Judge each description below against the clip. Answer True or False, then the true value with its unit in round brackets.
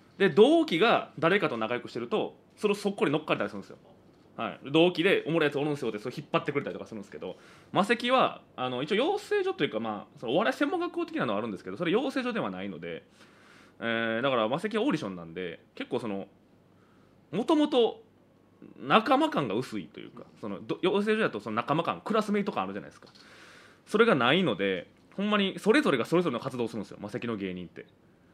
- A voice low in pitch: False (175 Hz)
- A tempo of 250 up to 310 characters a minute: False (470 characters per minute)